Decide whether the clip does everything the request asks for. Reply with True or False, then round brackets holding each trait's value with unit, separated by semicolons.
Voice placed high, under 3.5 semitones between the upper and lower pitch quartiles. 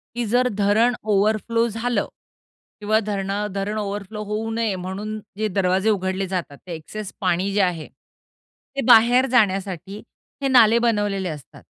True (205 Hz; 2.6 semitones)